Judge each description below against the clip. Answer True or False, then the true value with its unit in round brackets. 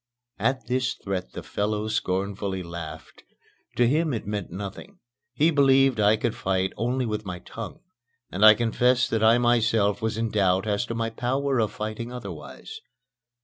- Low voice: True (110 Hz)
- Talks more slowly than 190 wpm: True (165 wpm)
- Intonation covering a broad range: False (3.4 semitones)